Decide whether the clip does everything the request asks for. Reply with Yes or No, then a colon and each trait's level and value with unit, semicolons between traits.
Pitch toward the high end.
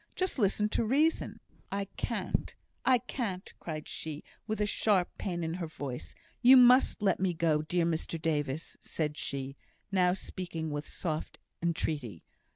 No: medium, 175 Hz